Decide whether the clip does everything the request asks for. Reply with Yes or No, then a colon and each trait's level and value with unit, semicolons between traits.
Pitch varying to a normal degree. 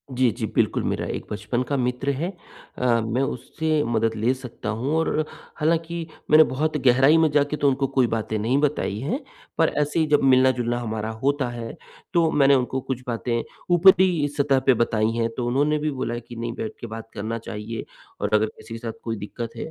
Yes: average, 4.5 semitones